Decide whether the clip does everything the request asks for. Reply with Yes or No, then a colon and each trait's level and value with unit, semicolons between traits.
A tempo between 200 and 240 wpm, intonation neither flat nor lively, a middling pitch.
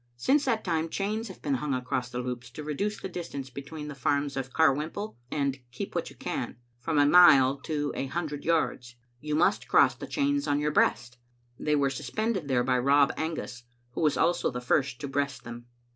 Yes: fast, 205 wpm; average, 3.9 semitones; medium, 145 Hz